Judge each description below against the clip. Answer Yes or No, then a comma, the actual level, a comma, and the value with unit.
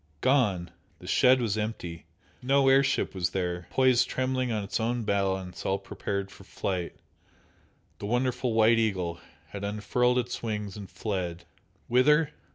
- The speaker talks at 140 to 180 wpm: Yes, average, 150 wpm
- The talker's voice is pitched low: Yes, low, 110 Hz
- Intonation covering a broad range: No, average, 4.7 semitones